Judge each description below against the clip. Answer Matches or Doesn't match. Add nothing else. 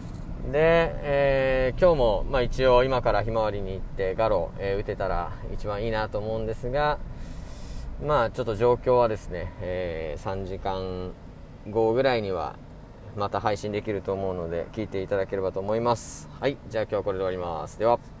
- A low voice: Matches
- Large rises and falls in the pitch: Doesn't match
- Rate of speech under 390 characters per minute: Matches